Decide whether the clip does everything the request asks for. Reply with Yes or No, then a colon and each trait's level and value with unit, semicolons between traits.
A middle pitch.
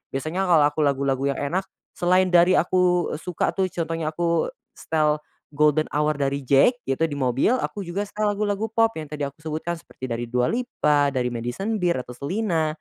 Yes: medium, 160 Hz